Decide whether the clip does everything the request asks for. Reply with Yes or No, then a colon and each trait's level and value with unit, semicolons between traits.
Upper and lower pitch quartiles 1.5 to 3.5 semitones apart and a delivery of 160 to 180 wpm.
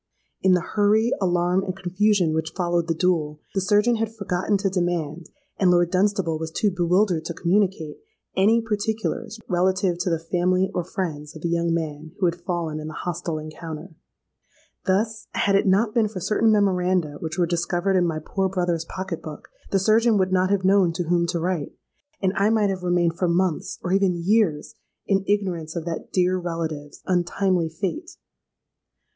Yes: average, 2.7 semitones; average, 175 wpm